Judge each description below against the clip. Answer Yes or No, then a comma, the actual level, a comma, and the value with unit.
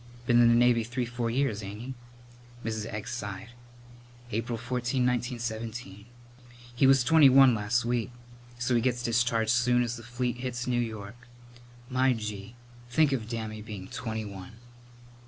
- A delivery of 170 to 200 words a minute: No, average, 155 wpm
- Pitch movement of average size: No, narrow, 2.0 semitones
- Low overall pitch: Yes, low, 120 Hz